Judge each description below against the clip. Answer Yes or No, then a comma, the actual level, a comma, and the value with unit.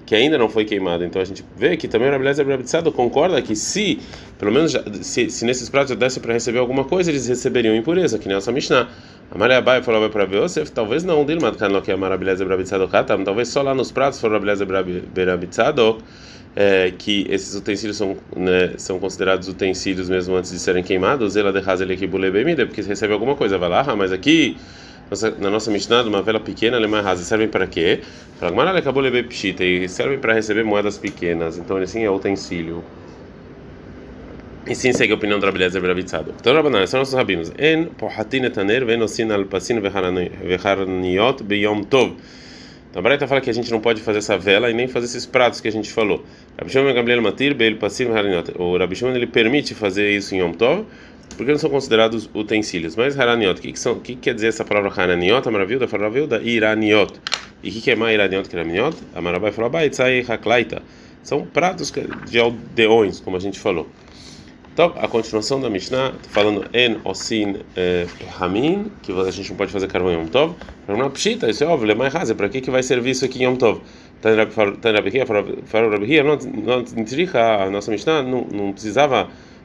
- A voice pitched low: Yes, low, 105 Hz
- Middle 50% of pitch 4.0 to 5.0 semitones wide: Yes, average, 4.3 semitones